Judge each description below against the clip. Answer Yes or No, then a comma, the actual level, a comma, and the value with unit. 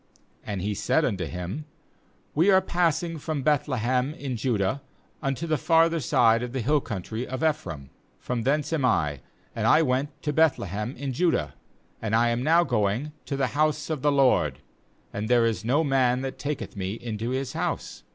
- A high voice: No, low, 130 Hz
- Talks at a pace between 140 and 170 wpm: No, average, 190 wpm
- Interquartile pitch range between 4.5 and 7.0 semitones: Yes, average, 5.2 semitones